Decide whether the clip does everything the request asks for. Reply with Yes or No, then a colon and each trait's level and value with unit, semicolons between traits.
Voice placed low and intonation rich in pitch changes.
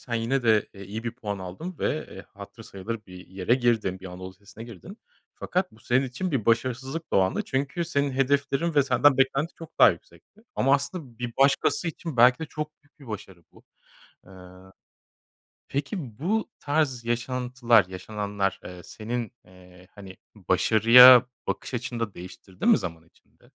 Yes: low, 120 Hz; wide, 5.8 semitones